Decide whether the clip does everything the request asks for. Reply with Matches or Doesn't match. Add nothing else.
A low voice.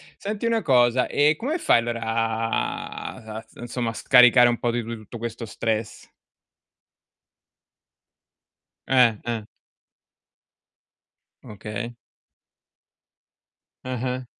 Matches